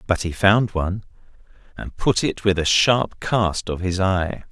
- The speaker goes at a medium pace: Yes, average, 185 wpm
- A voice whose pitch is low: Yes, very low, 95 Hz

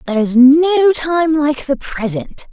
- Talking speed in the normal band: Yes, average, 165 wpm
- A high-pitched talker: Yes, very high, 285 Hz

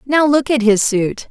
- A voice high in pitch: Yes, very high, 250 Hz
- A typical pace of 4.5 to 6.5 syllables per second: No, 4.2 syllables/s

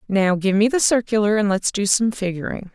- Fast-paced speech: Yes, fast, 220 wpm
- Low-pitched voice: No, high, 210 Hz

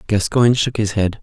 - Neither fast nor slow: Yes, average, 195 wpm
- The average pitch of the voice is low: Yes, low, 110 Hz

